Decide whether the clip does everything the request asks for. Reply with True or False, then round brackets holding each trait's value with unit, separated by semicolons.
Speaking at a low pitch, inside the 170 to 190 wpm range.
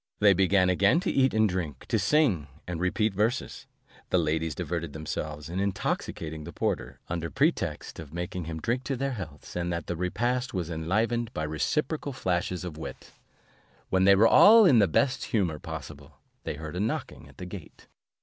True (90 Hz; 180 wpm)